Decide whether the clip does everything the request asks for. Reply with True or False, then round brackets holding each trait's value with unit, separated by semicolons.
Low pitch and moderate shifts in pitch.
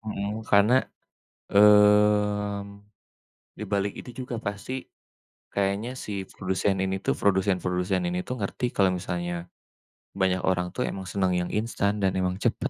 False (100 Hz; 1.8 semitones)